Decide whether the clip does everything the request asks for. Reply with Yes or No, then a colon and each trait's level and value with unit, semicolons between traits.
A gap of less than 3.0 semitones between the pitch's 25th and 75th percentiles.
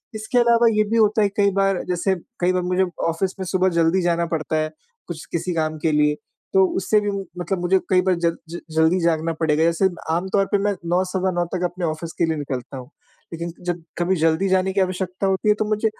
Yes: narrow, 2.6 semitones